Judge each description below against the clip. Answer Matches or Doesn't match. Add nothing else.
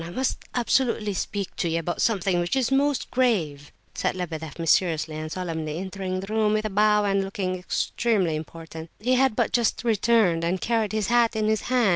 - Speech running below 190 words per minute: Doesn't match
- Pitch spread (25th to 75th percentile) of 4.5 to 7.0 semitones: Matches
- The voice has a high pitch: Matches